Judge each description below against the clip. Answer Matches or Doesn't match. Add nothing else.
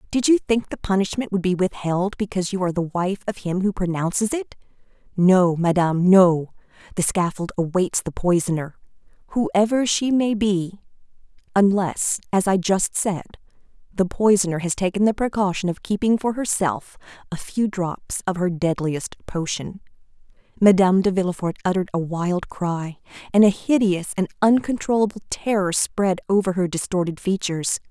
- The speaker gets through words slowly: Doesn't match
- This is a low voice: Doesn't match